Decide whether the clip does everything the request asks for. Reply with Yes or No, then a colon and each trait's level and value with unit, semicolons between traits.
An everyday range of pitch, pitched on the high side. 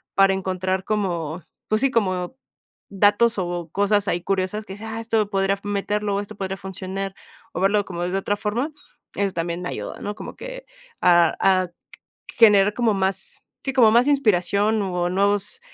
No: narrow, 2.2 semitones; high, 195 Hz